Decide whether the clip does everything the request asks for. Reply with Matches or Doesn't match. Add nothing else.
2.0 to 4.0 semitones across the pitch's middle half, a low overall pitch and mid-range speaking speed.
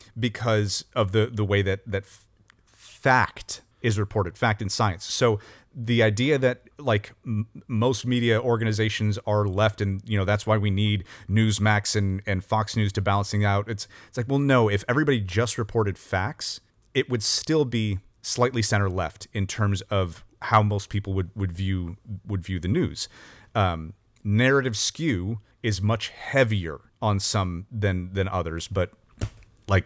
Matches